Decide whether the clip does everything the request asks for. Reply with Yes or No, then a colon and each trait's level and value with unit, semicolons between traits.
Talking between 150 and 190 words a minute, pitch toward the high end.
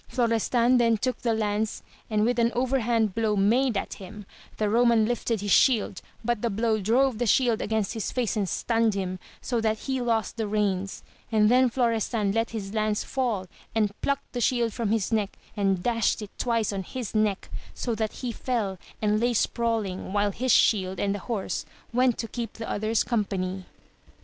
Yes: average, 185 wpm; high, 220 Hz